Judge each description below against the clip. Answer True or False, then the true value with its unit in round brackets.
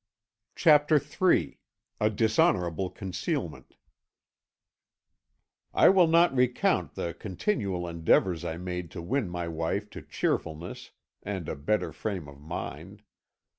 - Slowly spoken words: True (115 wpm)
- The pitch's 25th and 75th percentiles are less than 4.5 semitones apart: False (4.8 semitones)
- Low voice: True (95 Hz)